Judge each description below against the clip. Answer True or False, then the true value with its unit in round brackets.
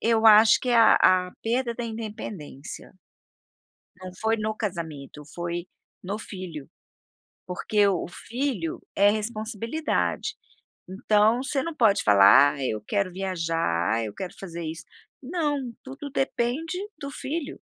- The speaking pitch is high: True (210 Hz)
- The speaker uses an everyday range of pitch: False (5.8 semitones)